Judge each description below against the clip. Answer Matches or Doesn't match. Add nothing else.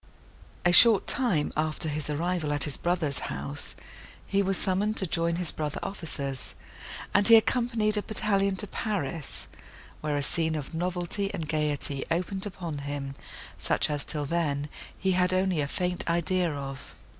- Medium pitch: Matches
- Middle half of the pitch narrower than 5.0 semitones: Matches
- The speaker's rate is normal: Matches